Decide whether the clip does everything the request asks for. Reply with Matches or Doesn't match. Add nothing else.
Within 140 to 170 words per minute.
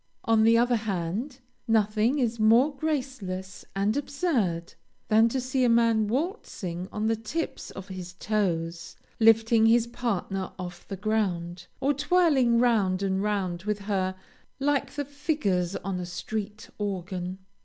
Matches